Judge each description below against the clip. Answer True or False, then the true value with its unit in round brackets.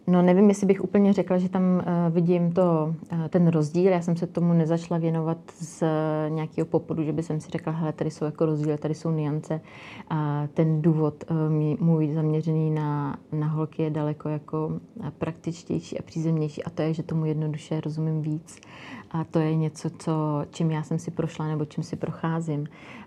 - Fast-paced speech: True (175 wpm)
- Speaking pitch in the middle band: True (160 Hz)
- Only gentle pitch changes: True (1.4 semitones)